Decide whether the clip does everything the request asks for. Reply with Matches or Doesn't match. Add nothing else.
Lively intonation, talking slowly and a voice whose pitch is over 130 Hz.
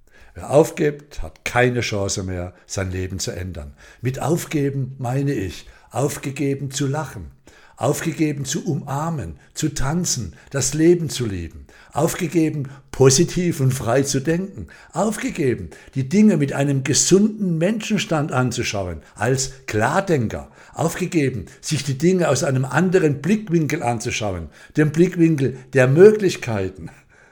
Matches